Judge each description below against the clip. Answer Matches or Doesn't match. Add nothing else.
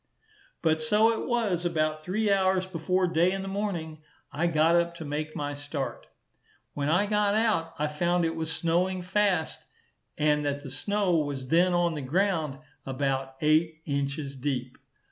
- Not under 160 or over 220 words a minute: Matches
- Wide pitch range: Doesn't match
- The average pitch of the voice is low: Doesn't match